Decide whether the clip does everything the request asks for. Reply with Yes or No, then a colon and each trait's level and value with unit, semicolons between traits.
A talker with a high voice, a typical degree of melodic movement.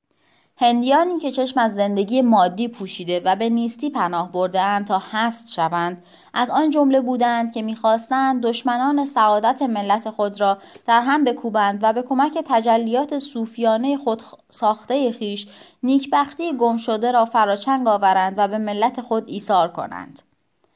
Yes: high, 230 Hz; average, 3.8 semitones